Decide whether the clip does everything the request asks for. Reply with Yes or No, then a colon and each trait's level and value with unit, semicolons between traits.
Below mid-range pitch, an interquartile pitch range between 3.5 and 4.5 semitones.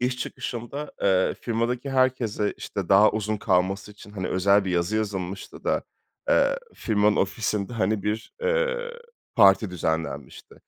Yes: low, 105 Hz; average, 3.9 semitones